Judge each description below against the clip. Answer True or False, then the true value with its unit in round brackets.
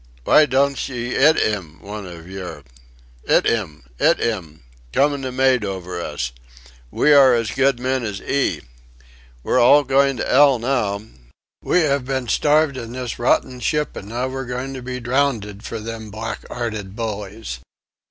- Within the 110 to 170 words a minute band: True (165 wpm)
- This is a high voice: False (120 Hz)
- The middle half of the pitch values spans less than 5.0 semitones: True (4.4 semitones)